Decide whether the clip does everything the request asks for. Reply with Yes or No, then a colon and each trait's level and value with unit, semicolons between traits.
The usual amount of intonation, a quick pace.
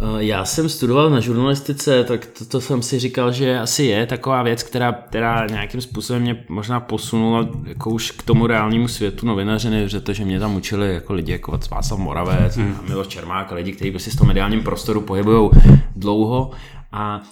Yes: average, 3.3 semitones; fast, 190 wpm